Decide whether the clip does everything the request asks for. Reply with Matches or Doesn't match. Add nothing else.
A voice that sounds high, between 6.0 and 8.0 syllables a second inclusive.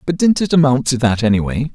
Doesn't match